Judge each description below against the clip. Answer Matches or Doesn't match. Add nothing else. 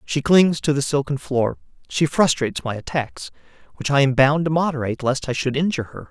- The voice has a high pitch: Doesn't match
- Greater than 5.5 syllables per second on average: Matches